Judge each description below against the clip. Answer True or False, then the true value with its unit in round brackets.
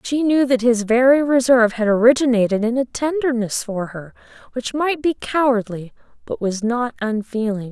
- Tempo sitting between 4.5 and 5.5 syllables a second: True (5.0 syllables/s)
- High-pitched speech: True (240 Hz)